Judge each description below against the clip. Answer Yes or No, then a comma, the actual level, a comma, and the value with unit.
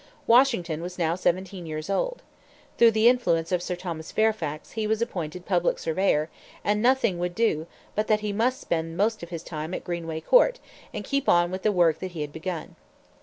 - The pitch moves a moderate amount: Yes, average, 4.7 semitones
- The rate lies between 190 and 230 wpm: Yes, fast, 205 wpm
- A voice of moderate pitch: Yes, medium, 180 Hz